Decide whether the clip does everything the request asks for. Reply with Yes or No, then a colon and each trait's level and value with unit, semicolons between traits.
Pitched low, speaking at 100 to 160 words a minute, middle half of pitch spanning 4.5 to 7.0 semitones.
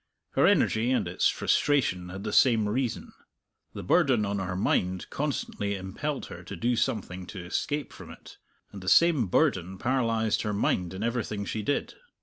No: low, 105 Hz; average, 170 wpm; average, 5.1 semitones